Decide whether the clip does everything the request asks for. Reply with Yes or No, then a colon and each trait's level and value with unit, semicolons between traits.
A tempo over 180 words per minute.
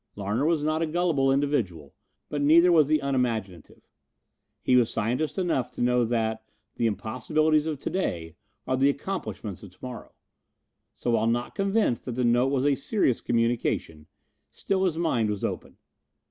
No: average, 165 wpm